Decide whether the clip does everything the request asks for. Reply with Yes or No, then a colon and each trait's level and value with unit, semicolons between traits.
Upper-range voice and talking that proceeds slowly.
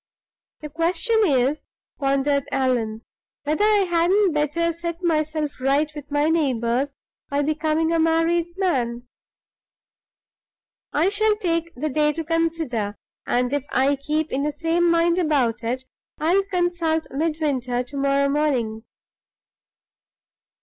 Yes: very high, 305 Hz; slow, 120 wpm